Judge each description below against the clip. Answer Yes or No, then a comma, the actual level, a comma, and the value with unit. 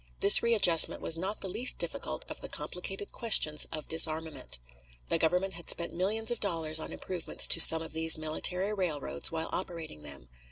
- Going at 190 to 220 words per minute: No, average, 175 wpm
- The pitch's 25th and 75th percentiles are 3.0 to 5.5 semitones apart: Yes, average, 3.3 semitones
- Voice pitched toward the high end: No, medium, 165 Hz